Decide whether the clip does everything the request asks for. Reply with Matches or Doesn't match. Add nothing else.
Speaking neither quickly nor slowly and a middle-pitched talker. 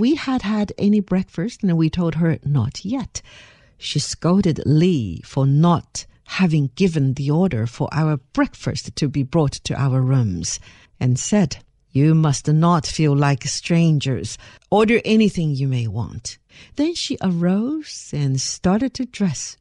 Matches